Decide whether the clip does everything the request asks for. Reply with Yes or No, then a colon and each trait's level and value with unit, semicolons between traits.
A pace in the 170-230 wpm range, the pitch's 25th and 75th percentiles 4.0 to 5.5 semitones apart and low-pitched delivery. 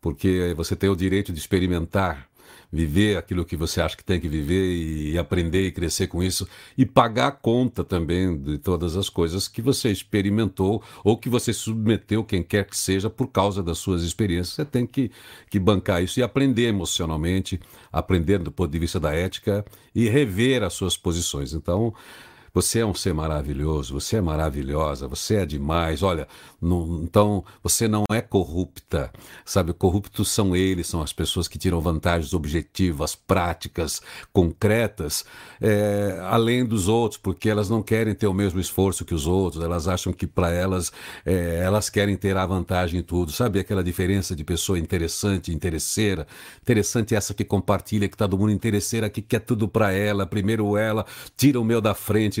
No: average, 180 wpm; average, 3.6 semitones; very low, 95 Hz